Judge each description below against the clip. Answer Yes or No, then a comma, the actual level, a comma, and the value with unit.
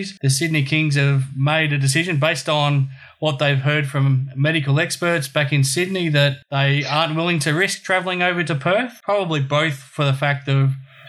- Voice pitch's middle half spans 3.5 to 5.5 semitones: No, average, 3.1 semitones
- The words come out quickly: No, average, 185 wpm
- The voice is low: No, medium, 150 Hz